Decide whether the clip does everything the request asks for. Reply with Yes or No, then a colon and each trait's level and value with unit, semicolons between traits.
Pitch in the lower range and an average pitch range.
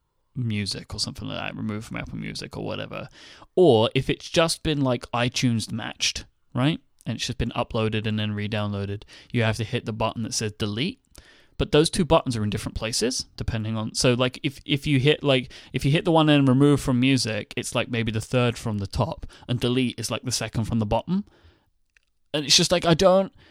Yes: low, 120 Hz; average, 4.2 semitones